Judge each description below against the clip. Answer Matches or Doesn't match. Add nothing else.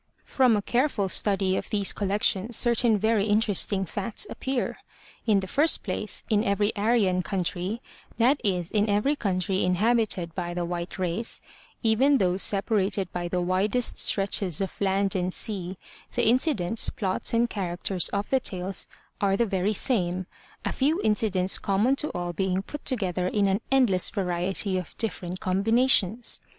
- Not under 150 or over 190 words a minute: Matches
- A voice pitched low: Doesn't match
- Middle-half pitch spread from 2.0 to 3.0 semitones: Doesn't match